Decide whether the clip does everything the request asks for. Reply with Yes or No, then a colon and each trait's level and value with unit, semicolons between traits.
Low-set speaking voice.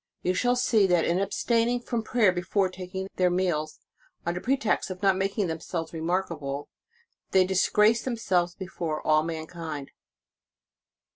No: medium, 185 Hz